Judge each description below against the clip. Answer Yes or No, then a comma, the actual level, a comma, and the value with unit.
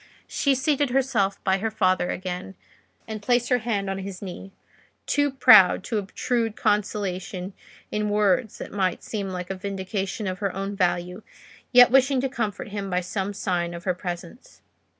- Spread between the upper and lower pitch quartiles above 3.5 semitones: No, average, 3.1 semitones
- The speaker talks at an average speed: Yes, average, 165 wpm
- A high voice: Yes, high, 200 Hz